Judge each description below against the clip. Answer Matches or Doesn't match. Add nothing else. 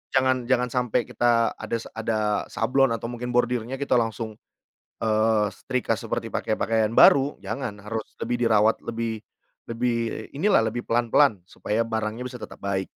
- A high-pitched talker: Doesn't match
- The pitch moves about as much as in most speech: Doesn't match